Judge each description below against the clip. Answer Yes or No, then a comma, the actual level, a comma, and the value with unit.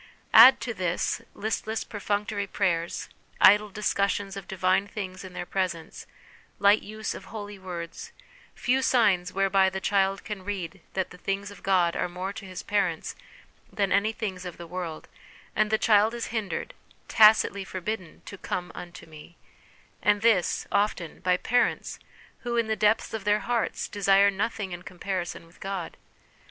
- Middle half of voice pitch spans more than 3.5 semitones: No, narrow, 2.4 semitones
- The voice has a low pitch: No, high, 195 Hz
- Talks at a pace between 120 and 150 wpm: No, average, 165 wpm